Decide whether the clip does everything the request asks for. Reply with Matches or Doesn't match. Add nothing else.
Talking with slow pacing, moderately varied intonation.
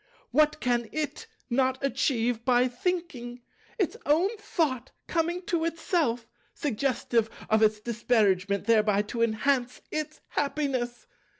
Matches